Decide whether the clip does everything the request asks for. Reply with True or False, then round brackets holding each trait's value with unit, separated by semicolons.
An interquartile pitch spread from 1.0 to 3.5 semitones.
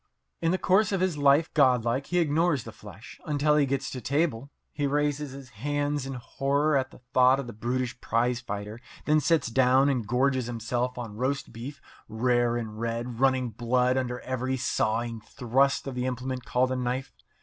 True (2.8 semitones)